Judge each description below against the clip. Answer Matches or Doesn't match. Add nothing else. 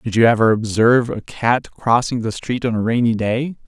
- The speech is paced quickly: Matches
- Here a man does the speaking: Matches